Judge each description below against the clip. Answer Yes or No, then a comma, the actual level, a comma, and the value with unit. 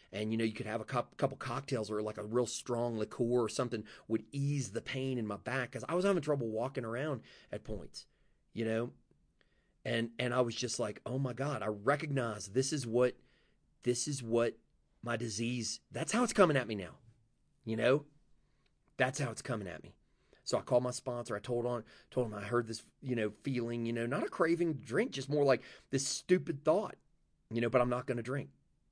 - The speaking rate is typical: No, fast, 220 wpm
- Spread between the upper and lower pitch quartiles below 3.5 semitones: Yes, average, 3.0 semitones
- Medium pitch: No, low, 125 Hz